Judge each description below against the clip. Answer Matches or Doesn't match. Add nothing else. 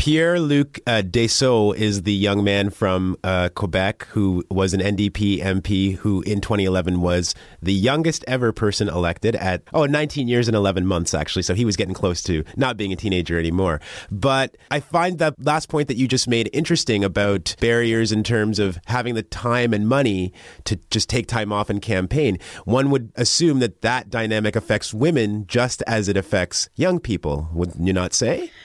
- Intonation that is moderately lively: Matches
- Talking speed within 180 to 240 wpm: Matches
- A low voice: Matches